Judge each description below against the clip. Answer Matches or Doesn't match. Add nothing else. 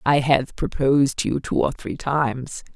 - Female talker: Matches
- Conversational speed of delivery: Matches